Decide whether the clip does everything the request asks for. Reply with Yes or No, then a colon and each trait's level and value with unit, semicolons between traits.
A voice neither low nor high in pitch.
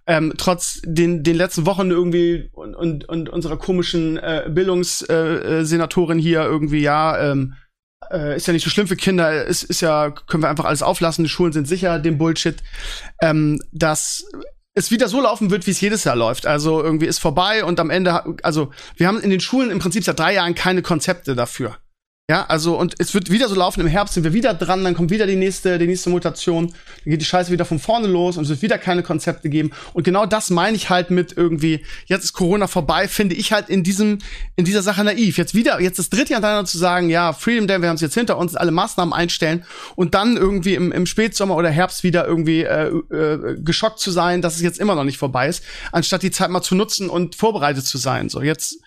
Yes: medium, 175 Hz